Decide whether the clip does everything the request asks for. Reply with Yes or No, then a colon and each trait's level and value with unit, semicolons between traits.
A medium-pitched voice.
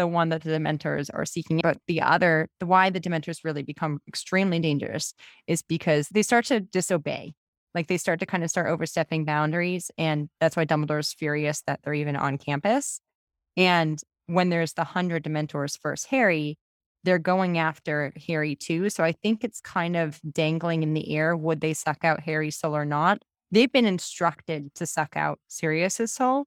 Yes: medium, 165 Hz